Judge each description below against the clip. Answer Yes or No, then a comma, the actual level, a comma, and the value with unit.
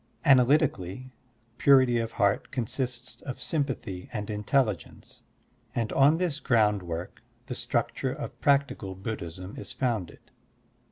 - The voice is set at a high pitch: No, low, 120 Hz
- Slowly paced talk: Yes, slow, 115 wpm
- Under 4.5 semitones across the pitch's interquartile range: No, average, 5.1 semitones